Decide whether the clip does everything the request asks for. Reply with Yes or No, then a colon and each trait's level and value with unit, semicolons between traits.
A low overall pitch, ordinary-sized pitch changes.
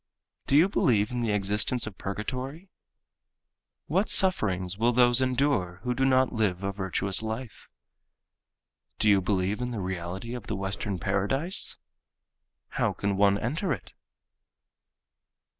Yes: low, 110 Hz; average, 4.8 semitones